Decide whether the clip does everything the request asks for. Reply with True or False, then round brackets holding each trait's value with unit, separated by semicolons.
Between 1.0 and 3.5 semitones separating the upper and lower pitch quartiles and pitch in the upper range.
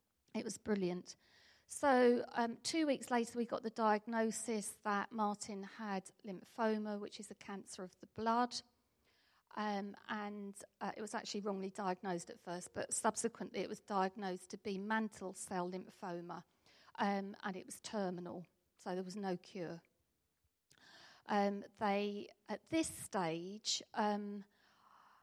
True (2.7 semitones; 205 Hz)